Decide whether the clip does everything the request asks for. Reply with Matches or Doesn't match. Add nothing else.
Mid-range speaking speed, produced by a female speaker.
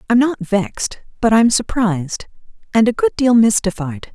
Matches